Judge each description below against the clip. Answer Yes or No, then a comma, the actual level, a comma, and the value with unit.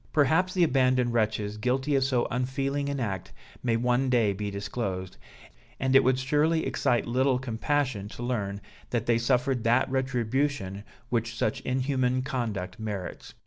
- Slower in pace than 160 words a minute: Yes, average, 150 wpm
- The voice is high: No, low, 125 Hz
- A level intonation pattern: No, average, 3.3 semitones